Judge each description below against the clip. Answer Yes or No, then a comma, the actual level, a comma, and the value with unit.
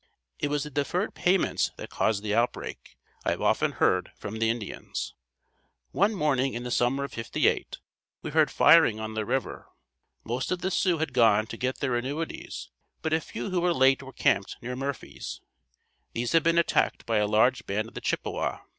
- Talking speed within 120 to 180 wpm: No, average, 190 wpm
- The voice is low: Yes, low, 130 Hz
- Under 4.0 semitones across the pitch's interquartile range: No, wide, 5.6 semitones